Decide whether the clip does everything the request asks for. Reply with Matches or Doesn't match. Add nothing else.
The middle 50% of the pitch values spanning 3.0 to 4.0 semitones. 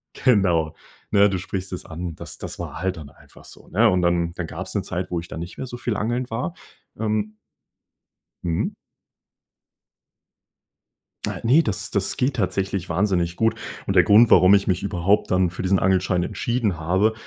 Matches